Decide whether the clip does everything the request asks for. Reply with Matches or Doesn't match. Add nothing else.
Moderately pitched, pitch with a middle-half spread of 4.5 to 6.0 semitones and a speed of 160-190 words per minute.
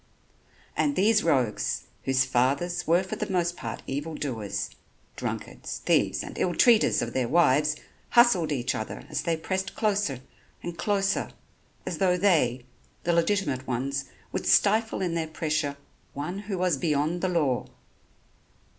Doesn't match